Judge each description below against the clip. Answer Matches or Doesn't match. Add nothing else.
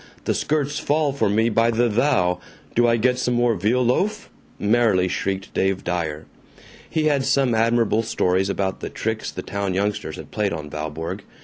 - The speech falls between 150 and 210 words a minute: Matches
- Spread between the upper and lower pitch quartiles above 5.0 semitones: Doesn't match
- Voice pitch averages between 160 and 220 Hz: Doesn't match